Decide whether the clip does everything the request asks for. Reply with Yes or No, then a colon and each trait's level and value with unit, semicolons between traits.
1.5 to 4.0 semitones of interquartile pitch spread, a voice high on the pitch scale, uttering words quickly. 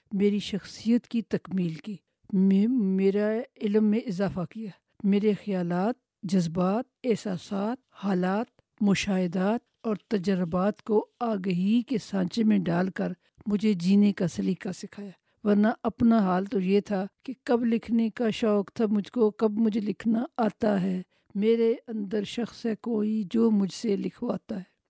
No: average, 2.7 semitones; high, 210 Hz; average, 145 wpm